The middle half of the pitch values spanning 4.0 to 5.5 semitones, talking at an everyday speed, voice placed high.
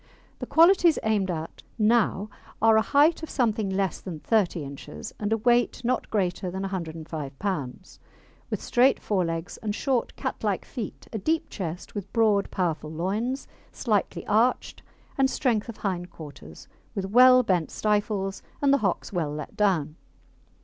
Yes: average, 5.0 semitones; average, 160 wpm; high, 200 Hz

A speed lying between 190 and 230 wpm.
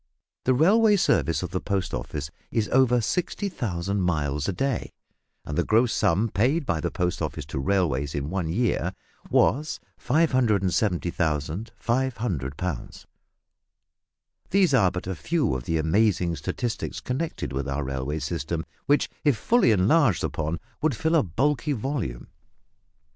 No: average, 140 wpm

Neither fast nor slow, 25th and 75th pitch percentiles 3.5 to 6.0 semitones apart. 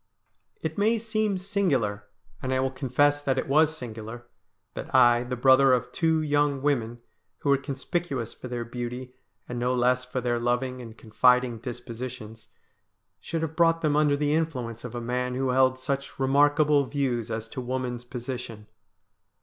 No: average, 165 wpm; average, 3.1 semitones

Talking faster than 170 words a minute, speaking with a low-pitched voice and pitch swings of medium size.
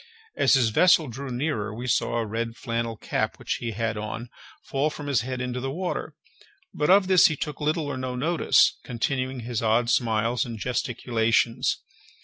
Yes: average, 180 wpm; low, 125 Hz; average, 3.6 semitones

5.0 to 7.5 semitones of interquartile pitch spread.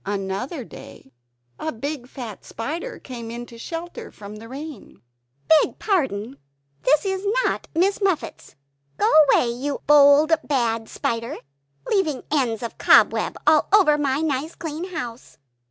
Yes: wide, 5.5 semitones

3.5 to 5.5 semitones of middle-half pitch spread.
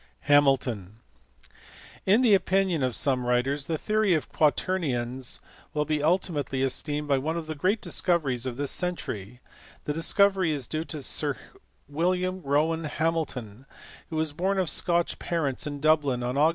Yes: average, 4.3 semitones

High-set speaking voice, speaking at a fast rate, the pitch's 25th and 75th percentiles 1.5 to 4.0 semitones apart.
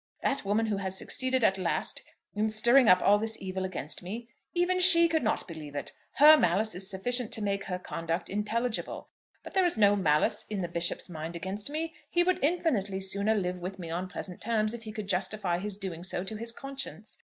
No: high, 205 Hz; fast, 210 wpm; average, 4.4 semitones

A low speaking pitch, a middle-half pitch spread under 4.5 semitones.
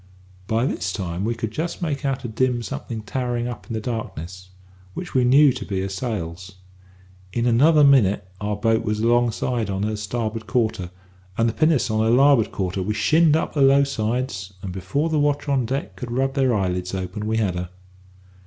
No: low, 115 Hz; average, 4.9 semitones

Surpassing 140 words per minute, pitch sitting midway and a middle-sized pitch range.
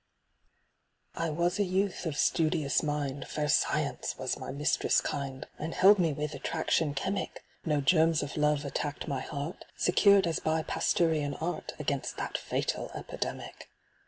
Yes: average, 150 wpm; medium, 155 Hz; average, 3.0 semitones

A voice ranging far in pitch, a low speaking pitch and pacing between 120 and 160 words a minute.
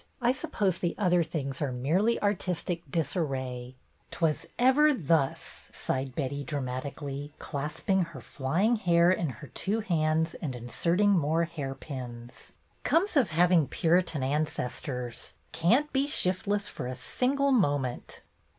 No: wide, 6.0 semitones; medium, 160 Hz; average, 140 wpm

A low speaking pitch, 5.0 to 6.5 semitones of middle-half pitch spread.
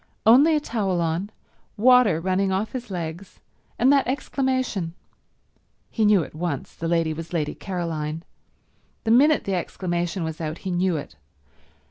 No: medium, 185 Hz; wide, 5.5 semitones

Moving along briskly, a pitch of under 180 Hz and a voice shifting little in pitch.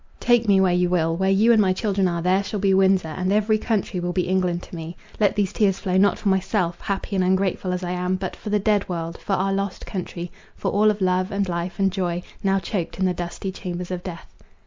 No: fast, 240 wpm; high, 190 Hz; narrow, 1.8 semitones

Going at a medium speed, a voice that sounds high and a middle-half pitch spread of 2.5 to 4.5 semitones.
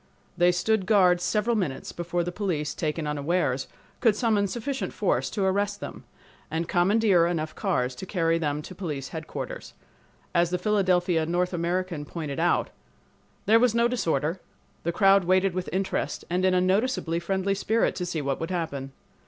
No: average, 170 wpm; medium, 180 Hz; average, 3.3 semitones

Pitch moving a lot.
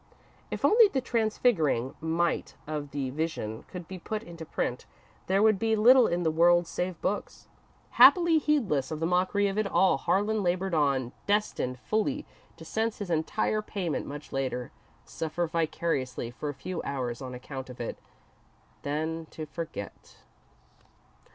Yes: wide, 6.4 semitones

